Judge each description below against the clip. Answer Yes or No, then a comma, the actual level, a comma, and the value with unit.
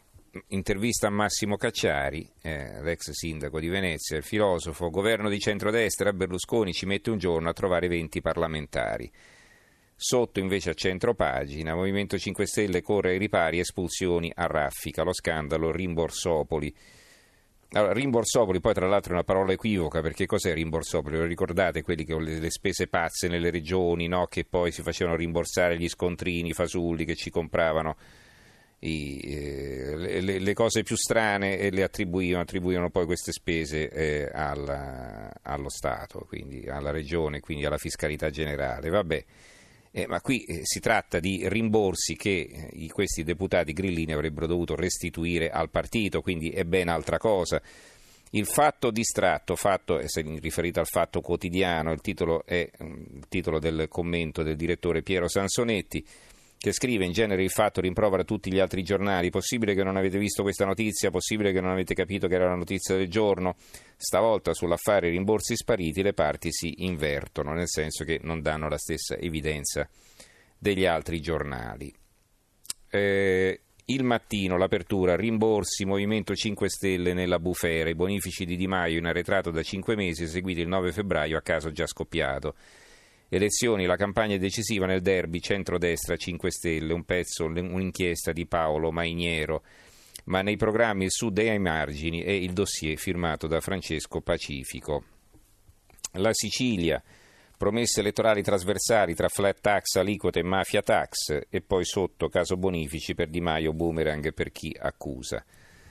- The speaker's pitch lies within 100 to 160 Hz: No, very low, 90 Hz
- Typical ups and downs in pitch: Yes, average, 3.3 semitones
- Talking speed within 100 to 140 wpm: No, average, 150 wpm